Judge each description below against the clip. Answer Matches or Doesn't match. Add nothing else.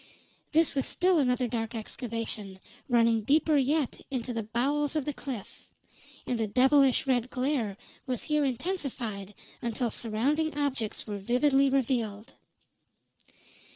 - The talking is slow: Matches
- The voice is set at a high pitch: Matches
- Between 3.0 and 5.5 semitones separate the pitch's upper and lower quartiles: Matches